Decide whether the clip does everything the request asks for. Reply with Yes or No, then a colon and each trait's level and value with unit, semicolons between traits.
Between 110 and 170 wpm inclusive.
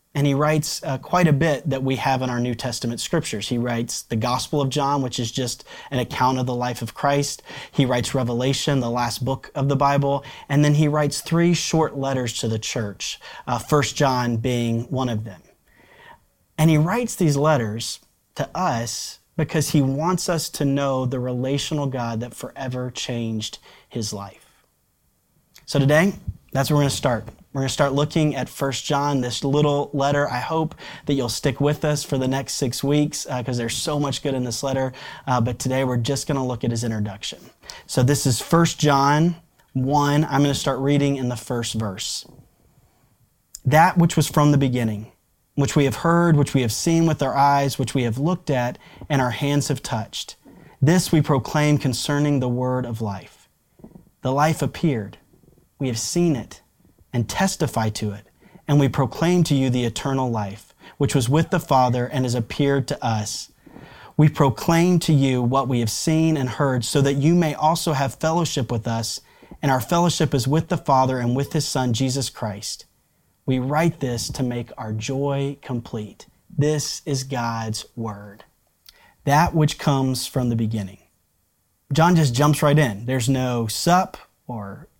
No: average, 190 wpm